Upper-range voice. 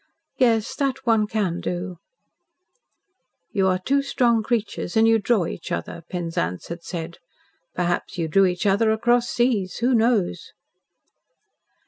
Yes: high, 210 Hz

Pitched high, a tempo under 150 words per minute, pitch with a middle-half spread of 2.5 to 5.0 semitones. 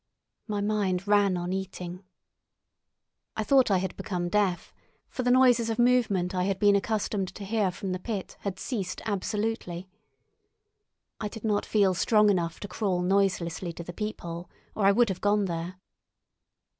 No: high, 200 Hz; average, 165 wpm; average, 2.8 semitones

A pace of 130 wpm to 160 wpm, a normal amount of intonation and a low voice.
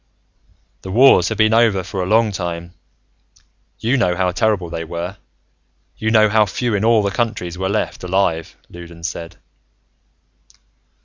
Yes: average, 150 wpm; average, 4.0 semitones; very low, 95 Hz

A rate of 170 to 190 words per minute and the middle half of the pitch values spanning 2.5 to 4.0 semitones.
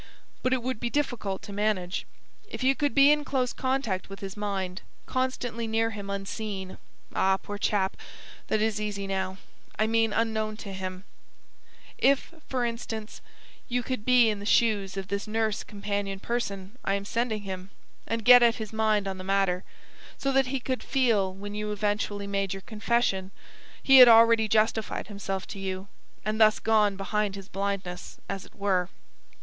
Yes: average, 175 wpm; average, 2.8 semitones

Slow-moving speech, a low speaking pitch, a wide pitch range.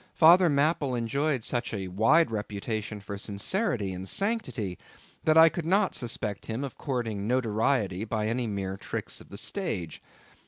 No: average, 155 wpm; low, 115 Hz; wide, 6.7 semitones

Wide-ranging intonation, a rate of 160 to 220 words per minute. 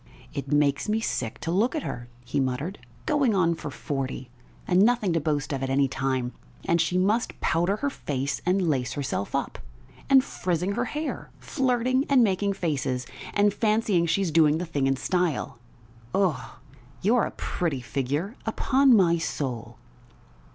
Yes: wide, 7.2 semitones; average, 165 wpm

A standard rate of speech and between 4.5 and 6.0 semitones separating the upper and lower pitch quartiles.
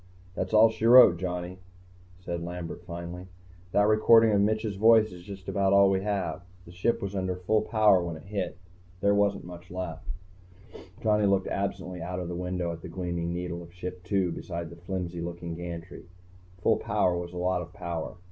No: average, 185 wpm; narrow, 2.4 semitones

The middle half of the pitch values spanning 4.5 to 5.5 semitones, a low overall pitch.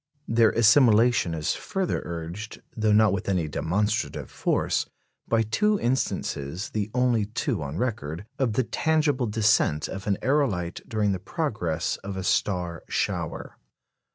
Yes: average, 5.2 semitones; low, 105 Hz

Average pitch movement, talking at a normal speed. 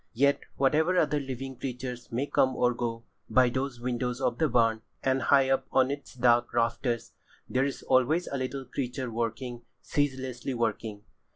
No: narrow, 2.0 semitones; average, 165 wpm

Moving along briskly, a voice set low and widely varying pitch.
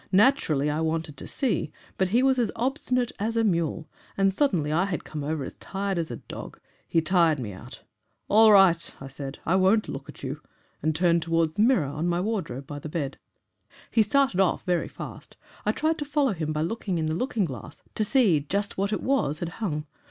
No: fast, 215 wpm; medium, 180 Hz; wide, 5.8 semitones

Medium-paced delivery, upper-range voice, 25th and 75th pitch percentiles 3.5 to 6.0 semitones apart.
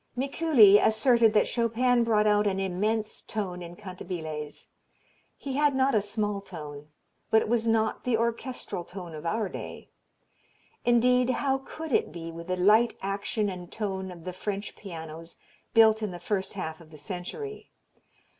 Yes: average, 165 wpm; high, 210 Hz; average, 4.5 semitones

